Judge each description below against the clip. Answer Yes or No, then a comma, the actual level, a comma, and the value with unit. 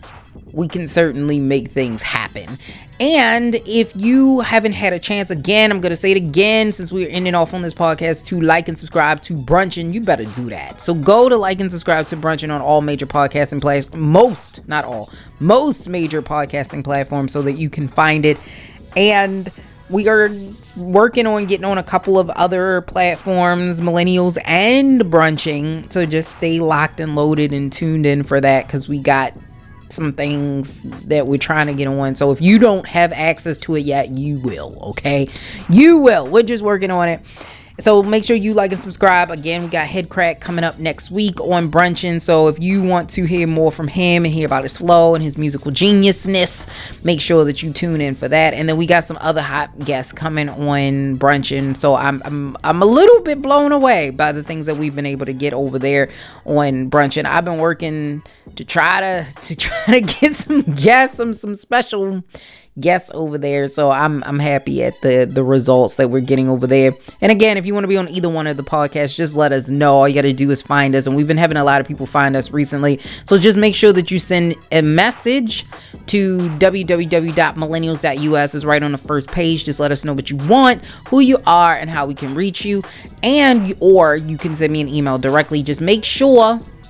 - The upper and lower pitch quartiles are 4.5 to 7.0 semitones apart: Yes, average, 4.8 semitones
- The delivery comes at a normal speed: No, fast, 215 wpm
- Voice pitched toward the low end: No, medium, 160 Hz